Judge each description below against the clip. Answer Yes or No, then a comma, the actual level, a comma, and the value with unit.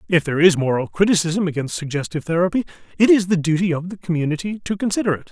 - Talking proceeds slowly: No, fast, 205 wpm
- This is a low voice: No, medium, 175 Hz